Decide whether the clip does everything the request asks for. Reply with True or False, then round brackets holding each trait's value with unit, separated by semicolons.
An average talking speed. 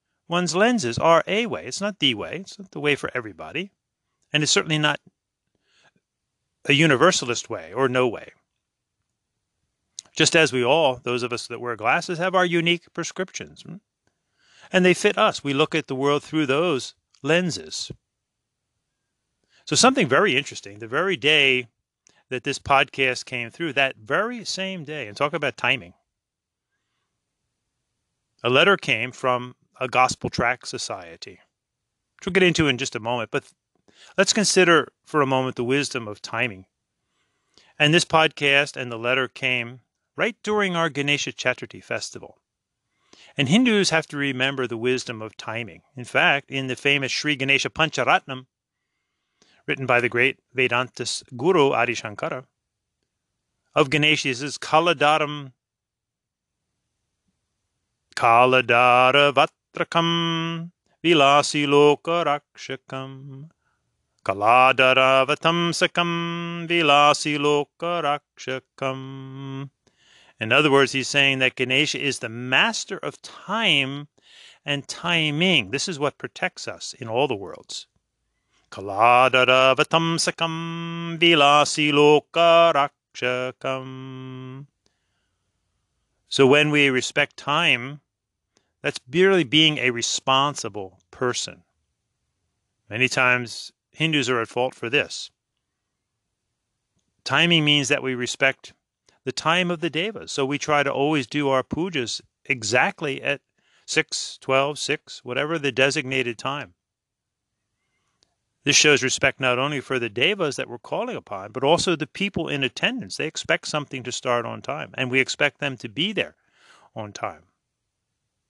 False (130 wpm)